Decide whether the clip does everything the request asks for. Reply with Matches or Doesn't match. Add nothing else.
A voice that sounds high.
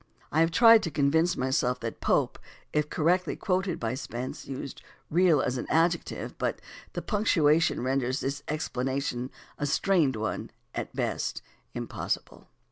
Doesn't match